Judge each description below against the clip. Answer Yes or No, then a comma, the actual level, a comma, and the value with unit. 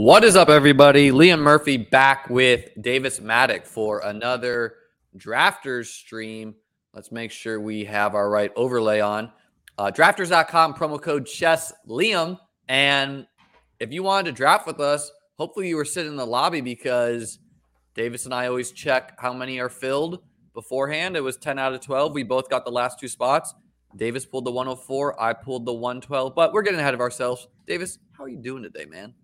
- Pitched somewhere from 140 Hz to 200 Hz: No, low, 130 Hz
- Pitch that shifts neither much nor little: Yes, average, 3.8 semitones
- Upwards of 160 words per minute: Yes, average, 185 wpm